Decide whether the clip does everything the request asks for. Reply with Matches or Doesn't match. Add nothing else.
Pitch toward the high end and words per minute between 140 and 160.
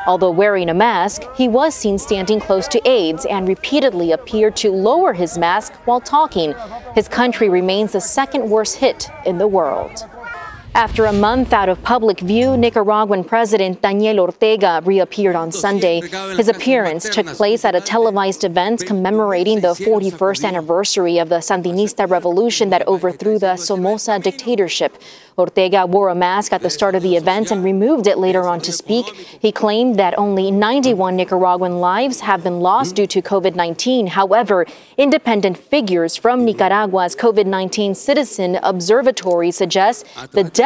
Matches